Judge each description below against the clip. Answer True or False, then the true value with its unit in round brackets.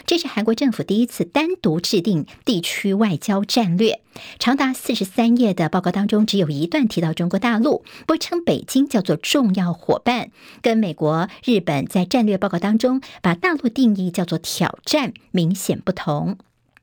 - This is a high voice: True (210 Hz)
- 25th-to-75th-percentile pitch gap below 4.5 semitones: False (5.1 semitones)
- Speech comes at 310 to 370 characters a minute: False (270 characters per minute)